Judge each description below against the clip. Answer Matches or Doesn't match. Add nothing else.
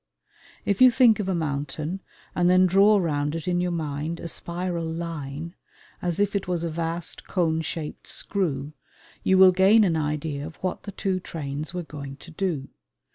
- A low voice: Doesn't match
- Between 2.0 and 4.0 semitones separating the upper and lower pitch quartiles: Matches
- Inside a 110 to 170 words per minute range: Doesn't match